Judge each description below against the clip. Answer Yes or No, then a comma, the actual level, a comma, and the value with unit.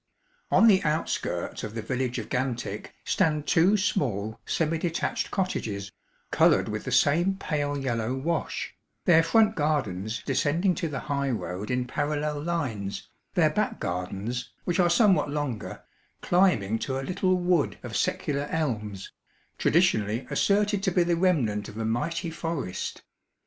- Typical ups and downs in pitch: No, wide, 7.1 semitones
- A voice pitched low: No, medium, 145 Hz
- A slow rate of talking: No, average, 145 wpm